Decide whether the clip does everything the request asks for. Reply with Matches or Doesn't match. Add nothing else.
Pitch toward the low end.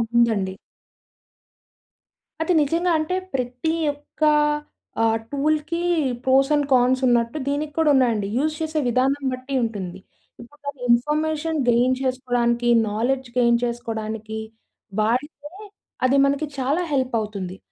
Doesn't match